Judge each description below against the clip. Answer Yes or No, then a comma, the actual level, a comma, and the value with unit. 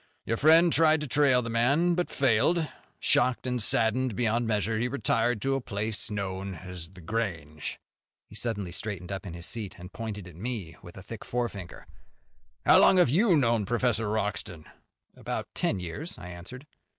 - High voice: No, low, 110 Hz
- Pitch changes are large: No, average, 4.8 semitones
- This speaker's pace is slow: No, average, 175 wpm